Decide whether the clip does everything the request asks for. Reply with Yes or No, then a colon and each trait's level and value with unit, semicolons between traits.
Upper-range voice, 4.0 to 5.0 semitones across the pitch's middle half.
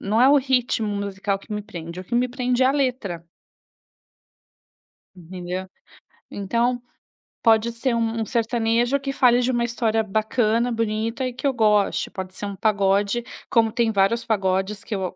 No: high, 225 Hz; average, 3.3 semitones